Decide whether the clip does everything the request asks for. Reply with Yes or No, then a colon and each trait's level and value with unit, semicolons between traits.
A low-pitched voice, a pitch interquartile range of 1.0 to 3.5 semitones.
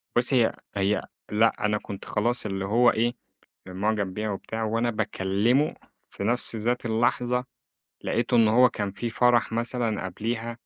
Yes: low, 115 Hz; narrow, 2.5 semitones